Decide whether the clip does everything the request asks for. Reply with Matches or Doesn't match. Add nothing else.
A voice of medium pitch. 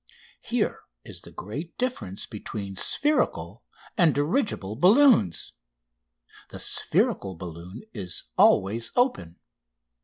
Doesn't match